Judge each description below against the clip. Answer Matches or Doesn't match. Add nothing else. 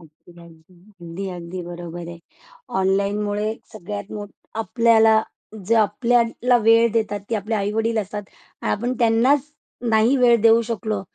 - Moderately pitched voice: Doesn't match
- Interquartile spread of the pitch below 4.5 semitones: Matches